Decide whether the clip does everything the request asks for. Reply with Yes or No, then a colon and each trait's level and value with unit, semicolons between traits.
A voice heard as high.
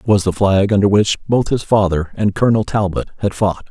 No: low, 100 Hz